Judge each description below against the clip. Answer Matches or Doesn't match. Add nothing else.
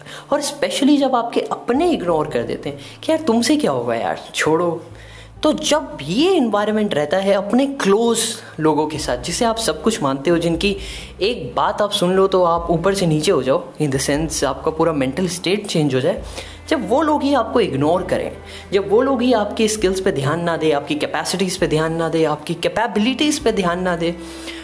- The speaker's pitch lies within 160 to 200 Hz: Matches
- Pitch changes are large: Matches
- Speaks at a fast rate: Matches